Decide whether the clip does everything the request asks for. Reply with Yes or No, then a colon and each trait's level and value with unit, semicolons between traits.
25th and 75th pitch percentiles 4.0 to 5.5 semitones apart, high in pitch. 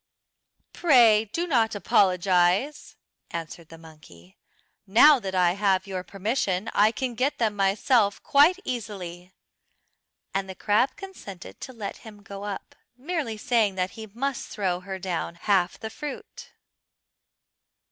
Yes: average, 4.5 semitones; high, 205 Hz